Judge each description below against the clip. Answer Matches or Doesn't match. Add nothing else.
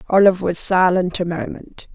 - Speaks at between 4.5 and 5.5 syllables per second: Matches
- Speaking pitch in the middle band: Matches